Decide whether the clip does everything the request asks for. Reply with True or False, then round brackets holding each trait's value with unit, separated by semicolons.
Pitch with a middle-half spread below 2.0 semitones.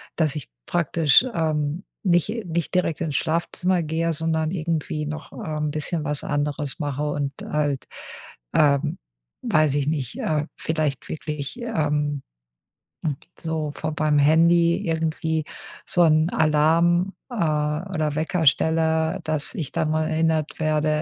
True (1.6 semitones)